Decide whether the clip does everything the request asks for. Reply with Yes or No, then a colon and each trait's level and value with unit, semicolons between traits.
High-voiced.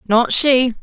Yes: high, 245 Hz